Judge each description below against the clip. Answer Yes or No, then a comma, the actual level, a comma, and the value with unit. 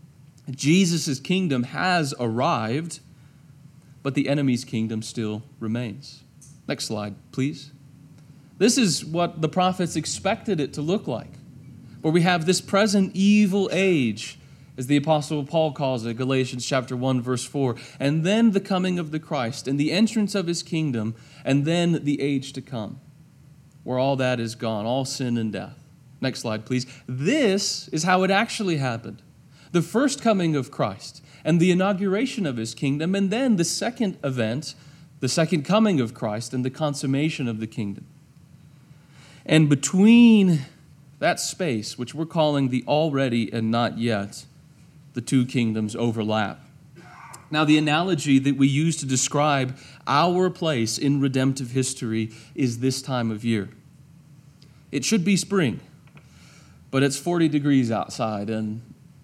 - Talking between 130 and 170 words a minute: Yes, average, 150 wpm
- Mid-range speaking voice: Yes, medium, 145 Hz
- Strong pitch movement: No, average, 4.2 semitones